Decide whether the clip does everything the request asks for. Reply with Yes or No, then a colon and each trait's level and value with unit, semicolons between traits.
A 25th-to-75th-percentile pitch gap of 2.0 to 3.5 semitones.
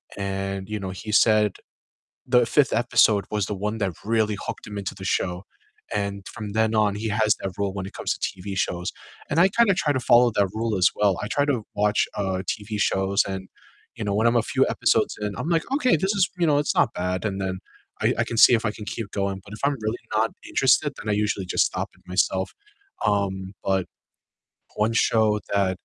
Yes: average, 2.7 semitones